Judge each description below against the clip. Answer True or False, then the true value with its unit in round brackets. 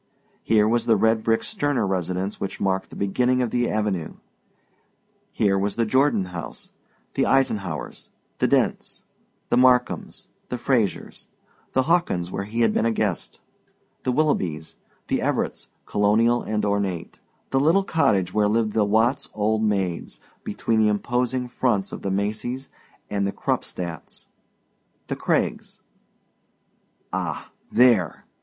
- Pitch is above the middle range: False (110 Hz)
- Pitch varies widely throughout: False (3.9 semitones)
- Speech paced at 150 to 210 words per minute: False (135 wpm)